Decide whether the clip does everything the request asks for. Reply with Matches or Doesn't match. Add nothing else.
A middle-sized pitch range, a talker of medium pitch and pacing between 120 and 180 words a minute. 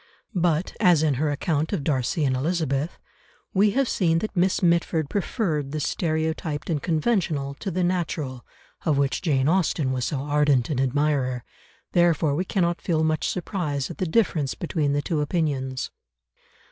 Matches